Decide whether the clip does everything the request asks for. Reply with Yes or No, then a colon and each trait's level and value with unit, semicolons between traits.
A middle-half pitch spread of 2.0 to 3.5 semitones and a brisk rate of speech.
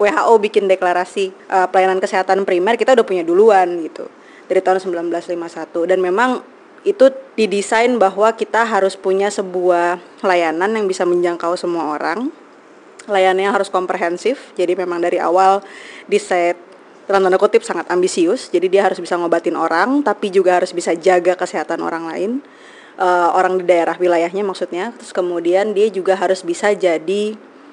Yes: average, 2.8 semitones; fast, 155 wpm